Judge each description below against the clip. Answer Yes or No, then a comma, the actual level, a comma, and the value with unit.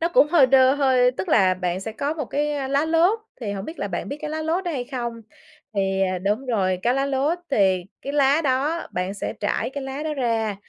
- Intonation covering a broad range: Yes, wide, 6.5 semitones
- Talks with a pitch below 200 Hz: No, very high, 265 Hz